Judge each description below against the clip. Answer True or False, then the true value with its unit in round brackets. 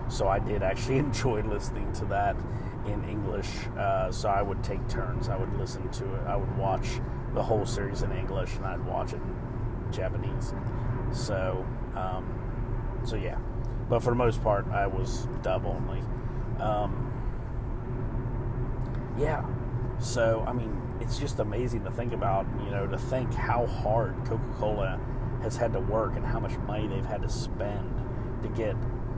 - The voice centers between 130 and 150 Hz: False (120 Hz)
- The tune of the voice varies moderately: False (1.8 semitones)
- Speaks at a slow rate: False (165 wpm)